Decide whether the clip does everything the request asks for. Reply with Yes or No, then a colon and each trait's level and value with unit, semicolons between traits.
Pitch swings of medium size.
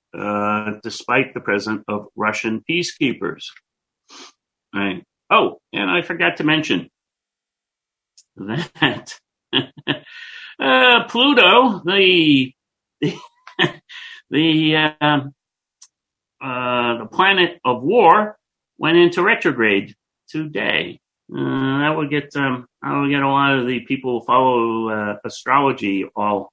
No: wide, 7.1 semitones